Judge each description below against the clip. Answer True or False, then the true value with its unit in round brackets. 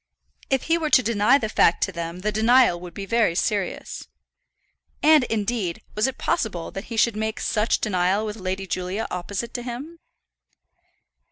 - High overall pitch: True (215 Hz)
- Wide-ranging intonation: False (4.2 semitones)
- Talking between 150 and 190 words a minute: True (170 wpm)